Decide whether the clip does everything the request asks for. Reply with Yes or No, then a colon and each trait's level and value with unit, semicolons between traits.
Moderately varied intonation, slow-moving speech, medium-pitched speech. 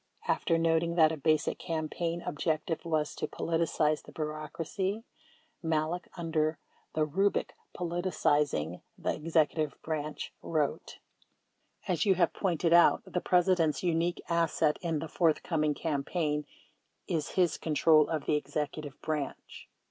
No: narrow, 1.9 semitones; slow, 125 wpm; medium, 160 Hz